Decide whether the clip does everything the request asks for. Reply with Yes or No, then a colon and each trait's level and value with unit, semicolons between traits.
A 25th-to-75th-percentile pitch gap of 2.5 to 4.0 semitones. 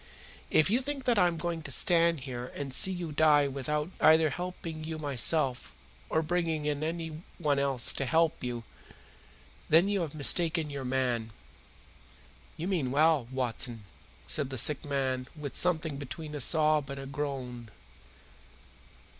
Yes: average, 3.4 semitones